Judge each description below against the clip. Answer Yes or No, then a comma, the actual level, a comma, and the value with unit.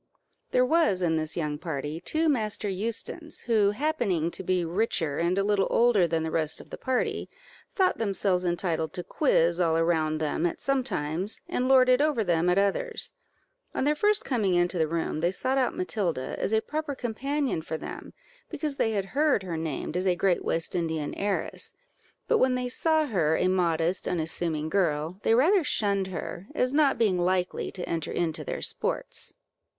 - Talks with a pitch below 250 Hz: Yes, high, 190 Hz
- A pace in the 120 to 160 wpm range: No, average, 185 wpm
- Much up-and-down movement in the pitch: Yes, wide, 7.2 semitones